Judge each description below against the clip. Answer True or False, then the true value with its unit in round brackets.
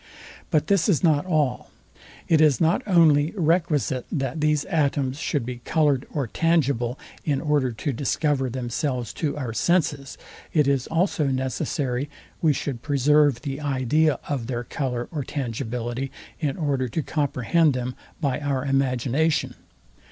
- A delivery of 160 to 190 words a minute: False (145 wpm)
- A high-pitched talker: False (140 Hz)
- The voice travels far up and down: False (3.1 semitones)